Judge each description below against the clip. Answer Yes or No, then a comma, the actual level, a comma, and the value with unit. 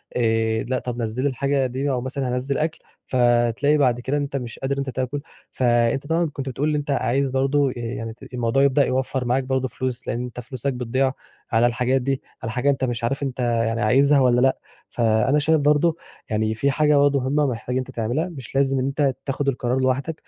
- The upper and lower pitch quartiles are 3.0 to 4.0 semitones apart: No, narrow, 2.4 semitones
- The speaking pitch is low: Yes, low, 130 Hz